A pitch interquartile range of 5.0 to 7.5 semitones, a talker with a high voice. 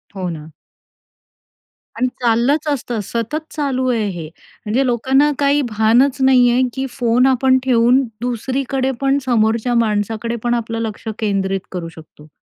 No: average, 3.3 semitones; high, 240 Hz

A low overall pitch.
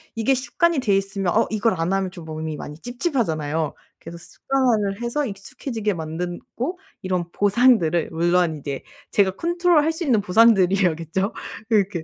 No: high, 195 Hz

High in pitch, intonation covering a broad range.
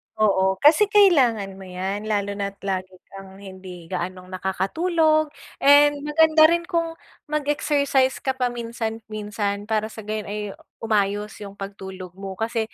Yes: high, 215 Hz; wide, 6.6 semitones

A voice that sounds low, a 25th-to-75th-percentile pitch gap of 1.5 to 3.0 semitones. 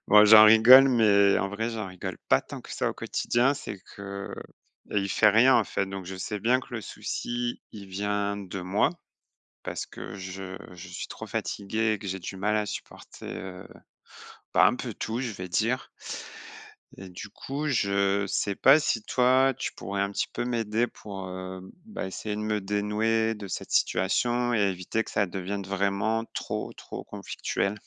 Yes: low, 105 Hz; narrow, 2.6 semitones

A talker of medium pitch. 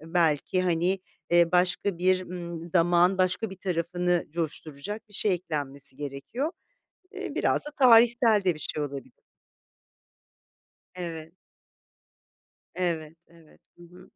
Yes: medium, 175 Hz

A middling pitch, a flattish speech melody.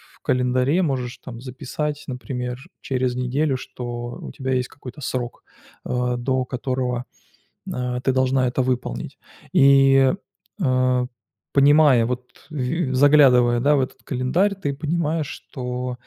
No: low, 130 Hz; narrow, 2.0 semitones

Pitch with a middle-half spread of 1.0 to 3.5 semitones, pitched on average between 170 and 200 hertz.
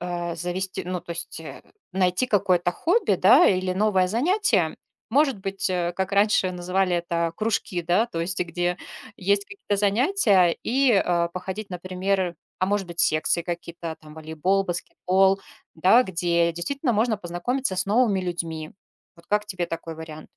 Yes: average, 3.0 semitones; medium, 185 Hz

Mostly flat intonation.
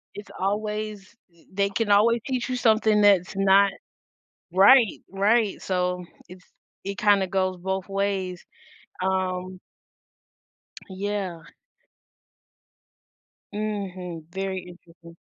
Yes: narrow, 2.1 semitones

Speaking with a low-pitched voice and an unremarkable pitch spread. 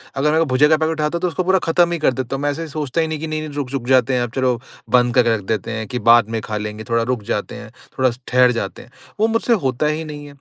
Yes: low, 130 Hz; average, 4.6 semitones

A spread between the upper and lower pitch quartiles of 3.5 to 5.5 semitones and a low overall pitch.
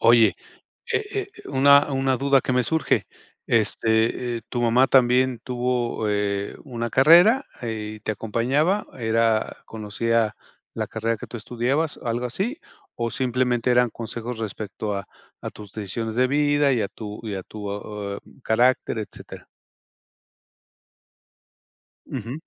No: average, 3.1 semitones; low, 120 Hz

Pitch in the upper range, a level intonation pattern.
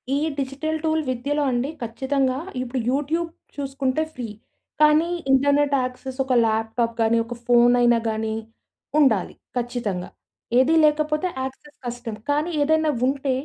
No: very high, 265 Hz; average, 3.5 semitones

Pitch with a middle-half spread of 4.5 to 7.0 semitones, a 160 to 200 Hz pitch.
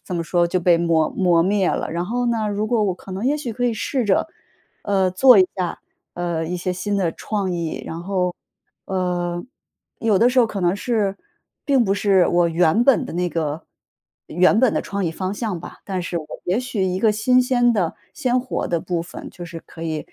No: average, 4.0 semitones; high, 190 Hz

